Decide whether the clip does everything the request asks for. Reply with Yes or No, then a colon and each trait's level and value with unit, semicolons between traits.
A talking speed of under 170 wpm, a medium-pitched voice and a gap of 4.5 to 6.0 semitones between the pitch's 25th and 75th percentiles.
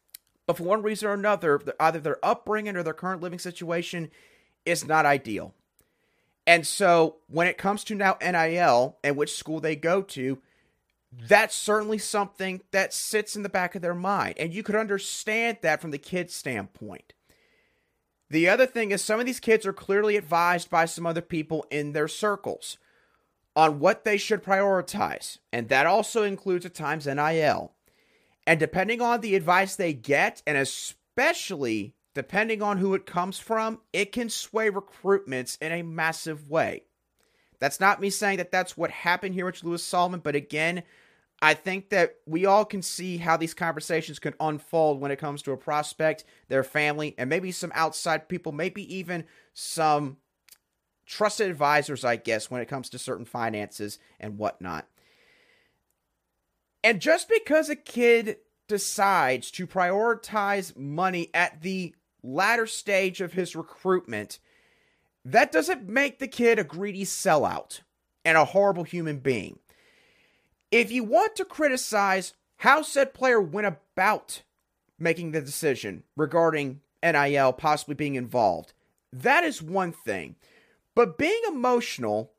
Yes: average, 155 wpm; medium, 180 Hz; average, 5.0 semitones